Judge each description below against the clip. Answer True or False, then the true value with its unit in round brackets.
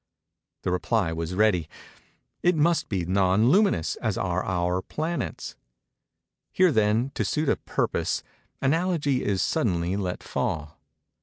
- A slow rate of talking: True (125 wpm)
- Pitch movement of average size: False (8.4 semitones)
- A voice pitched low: True (105 Hz)